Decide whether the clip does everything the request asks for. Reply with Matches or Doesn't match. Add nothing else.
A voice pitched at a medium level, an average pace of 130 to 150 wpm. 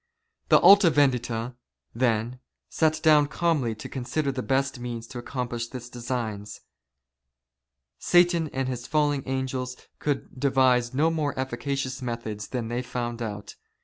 Doesn't match